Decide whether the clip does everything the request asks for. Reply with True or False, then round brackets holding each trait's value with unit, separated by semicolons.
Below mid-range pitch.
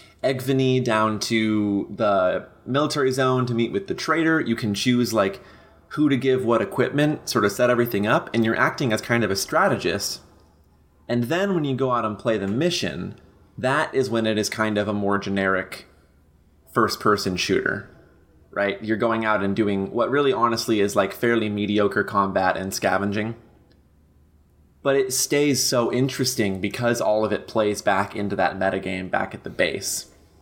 True (110 Hz)